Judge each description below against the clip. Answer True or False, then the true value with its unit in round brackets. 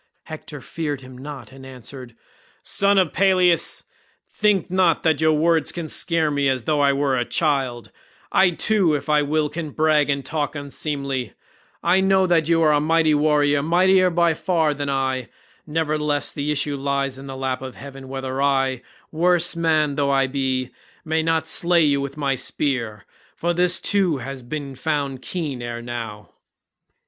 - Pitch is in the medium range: True (145 Hz)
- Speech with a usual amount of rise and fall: True (3.4 semitones)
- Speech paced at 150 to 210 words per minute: True (175 wpm)